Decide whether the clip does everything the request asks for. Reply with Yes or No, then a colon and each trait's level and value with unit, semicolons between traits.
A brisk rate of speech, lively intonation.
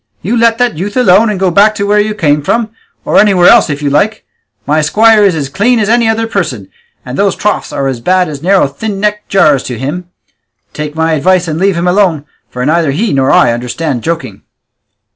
Yes: fast, 220 wpm; wide, 6.0 semitones